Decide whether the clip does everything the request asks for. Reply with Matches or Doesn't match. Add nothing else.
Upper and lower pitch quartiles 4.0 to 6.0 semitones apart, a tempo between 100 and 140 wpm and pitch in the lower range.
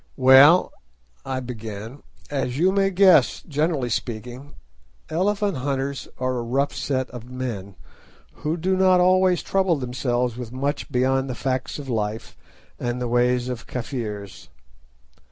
Doesn't match